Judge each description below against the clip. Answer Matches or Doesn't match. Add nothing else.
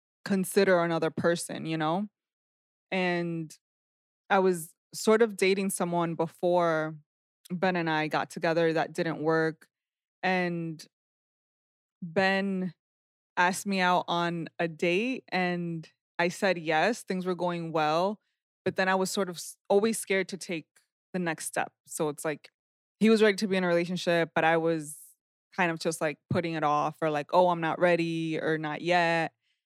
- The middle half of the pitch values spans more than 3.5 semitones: Doesn't match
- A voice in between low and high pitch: Matches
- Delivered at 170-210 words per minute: Doesn't match